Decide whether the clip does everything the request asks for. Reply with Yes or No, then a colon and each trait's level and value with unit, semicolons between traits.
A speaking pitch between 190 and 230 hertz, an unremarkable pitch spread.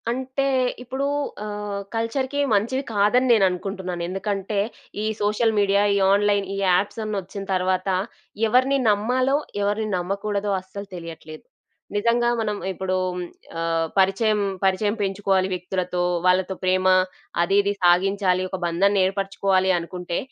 No: high, 200 Hz; narrow, 2.3 semitones